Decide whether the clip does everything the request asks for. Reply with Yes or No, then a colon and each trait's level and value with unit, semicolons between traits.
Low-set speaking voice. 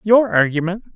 No: high, 190 Hz